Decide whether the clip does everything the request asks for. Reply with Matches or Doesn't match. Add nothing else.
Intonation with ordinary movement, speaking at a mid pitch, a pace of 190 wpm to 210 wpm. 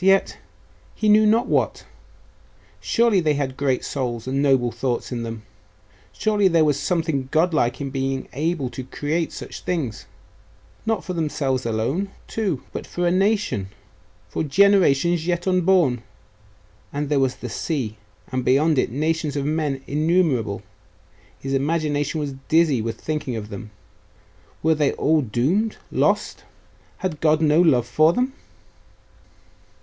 Doesn't match